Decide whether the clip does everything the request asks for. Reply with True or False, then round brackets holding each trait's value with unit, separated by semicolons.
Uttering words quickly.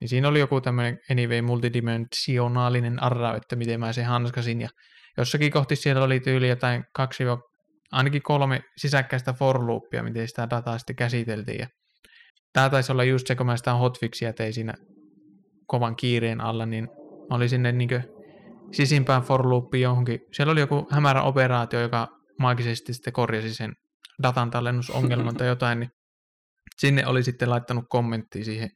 True (160 wpm)